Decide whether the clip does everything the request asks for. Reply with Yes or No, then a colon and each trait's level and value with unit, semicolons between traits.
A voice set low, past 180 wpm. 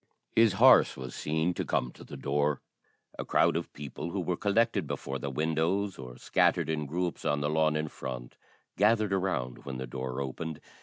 Yes: very low, 75 Hz; average, 190 wpm